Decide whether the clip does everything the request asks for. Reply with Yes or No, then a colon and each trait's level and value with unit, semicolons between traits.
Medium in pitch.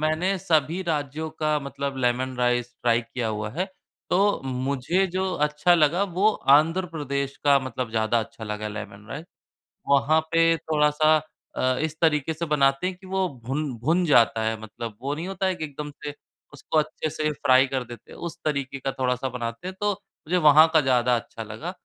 Yes: medium, 145 Hz